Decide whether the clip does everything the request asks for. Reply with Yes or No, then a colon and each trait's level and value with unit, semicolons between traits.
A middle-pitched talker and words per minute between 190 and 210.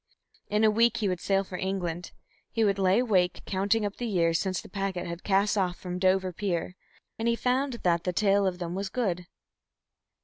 No: high, 195 Hz; average, 200 wpm